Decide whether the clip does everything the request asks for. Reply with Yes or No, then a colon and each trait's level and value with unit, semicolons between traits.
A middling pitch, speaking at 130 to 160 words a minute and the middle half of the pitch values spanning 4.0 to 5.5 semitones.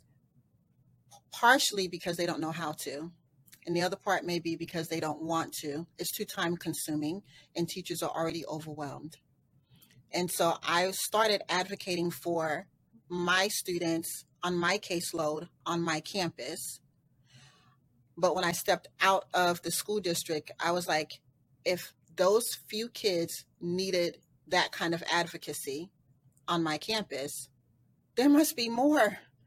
No: medium, 170 Hz; average, 140 wpm; average, 3.1 semitones